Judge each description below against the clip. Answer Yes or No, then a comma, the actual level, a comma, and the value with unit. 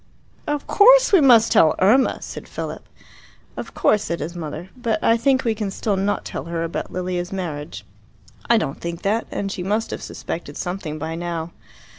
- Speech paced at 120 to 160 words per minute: No, average, 185 wpm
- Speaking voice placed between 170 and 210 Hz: Yes, high, 190 Hz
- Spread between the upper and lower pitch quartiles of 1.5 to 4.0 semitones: No, average, 5.1 semitones